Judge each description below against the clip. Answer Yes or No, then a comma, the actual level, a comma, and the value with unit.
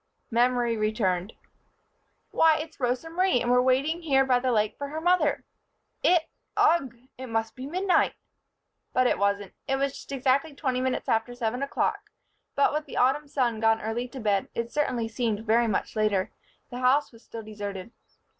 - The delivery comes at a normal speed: Yes, average, 175 wpm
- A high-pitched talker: Yes, very high, 250 Hz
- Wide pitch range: No, average, 3.9 semitones